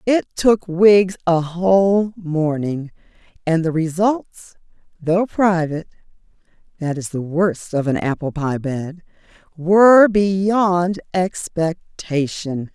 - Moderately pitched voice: Yes, medium, 175 Hz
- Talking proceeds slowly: Yes, slow, 110 wpm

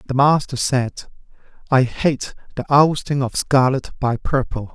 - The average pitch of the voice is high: No, low, 135 Hz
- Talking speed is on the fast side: No, average, 140 wpm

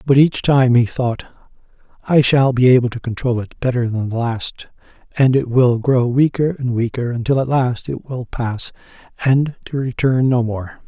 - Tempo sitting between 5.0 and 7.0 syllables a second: No, 4.5 syllables/s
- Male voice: Yes, male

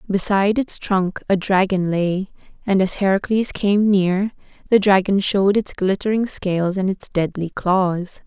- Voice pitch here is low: No, high, 195 Hz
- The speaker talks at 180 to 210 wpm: No, average, 150 wpm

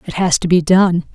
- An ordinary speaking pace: No, fast, 260 wpm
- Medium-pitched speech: Yes, medium, 180 Hz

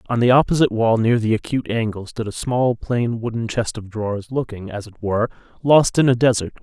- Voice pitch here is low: Yes, low, 115 Hz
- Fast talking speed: Yes, fast, 215 wpm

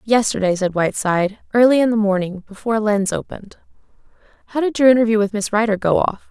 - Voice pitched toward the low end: No, high, 215 Hz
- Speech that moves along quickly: No, average, 180 wpm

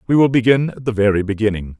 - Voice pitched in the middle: No, low, 115 Hz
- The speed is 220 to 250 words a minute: Yes, fast, 235 wpm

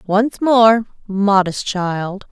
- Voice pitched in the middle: No, high, 205 Hz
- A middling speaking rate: No, slow, 105 wpm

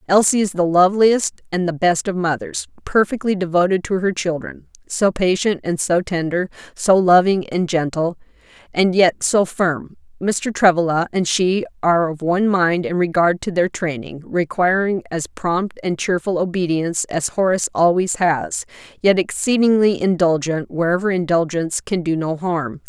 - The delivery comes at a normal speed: Yes, average, 155 wpm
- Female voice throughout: Yes, female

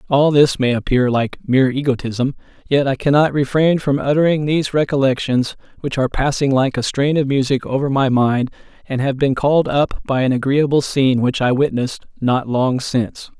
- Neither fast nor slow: Yes, average, 185 wpm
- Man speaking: Yes, male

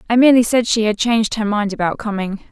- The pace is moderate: No, fast, 240 wpm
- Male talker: No, female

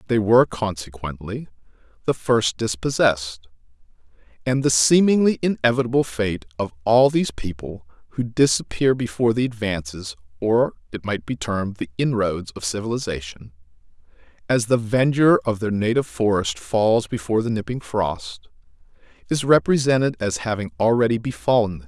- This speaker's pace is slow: Yes, slow, 130 wpm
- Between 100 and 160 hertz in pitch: Yes, low, 110 Hz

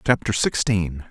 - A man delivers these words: Yes, male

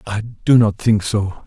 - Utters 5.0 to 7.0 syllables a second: No, 4.4 syllables/s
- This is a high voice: No, low, 105 Hz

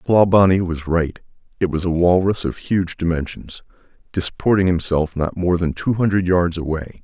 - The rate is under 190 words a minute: Yes, average, 160 wpm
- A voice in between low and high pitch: No, very low, 90 Hz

